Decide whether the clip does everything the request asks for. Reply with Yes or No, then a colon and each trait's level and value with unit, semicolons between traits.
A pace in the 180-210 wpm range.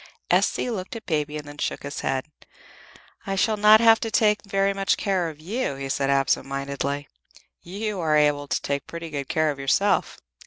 Yes: average, 195 wpm